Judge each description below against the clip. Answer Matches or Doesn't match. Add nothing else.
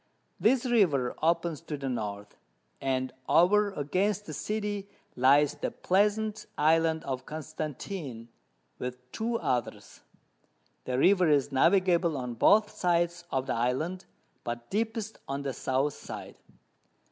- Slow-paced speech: Matches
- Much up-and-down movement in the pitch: Matches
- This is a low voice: Doesn't match